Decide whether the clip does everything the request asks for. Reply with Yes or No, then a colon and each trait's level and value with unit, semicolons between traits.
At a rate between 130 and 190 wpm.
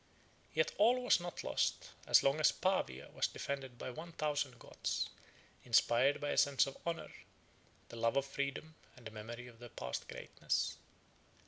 Yes: average, 165 wpm